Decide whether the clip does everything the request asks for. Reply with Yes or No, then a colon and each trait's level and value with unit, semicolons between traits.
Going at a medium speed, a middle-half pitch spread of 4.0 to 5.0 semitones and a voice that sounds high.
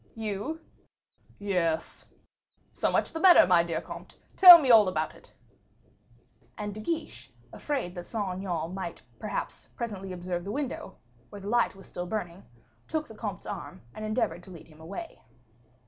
Yes: average, 165 wpm; average, 4.6 semitones; high, 200 Hz